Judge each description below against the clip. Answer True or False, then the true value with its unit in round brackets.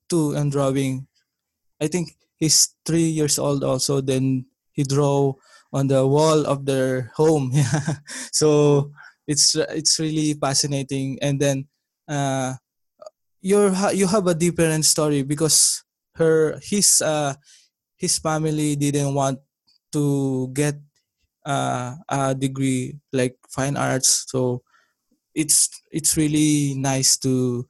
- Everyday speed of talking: False (115 wpm)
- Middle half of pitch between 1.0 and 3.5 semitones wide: True (2.5 semitones)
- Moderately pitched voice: True (145 Hz)